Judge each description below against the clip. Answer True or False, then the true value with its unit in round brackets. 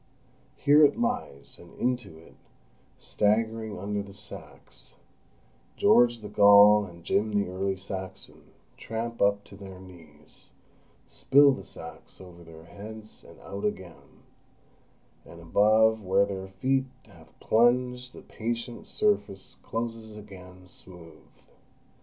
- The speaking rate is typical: False (125 wpm)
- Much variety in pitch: False (3.4 semitones)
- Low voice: True (100 Hz)